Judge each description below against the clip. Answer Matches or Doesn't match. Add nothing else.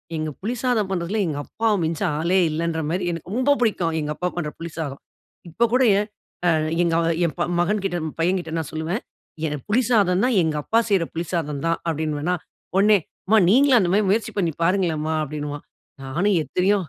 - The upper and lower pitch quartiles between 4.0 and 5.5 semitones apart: Matches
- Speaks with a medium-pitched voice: Matches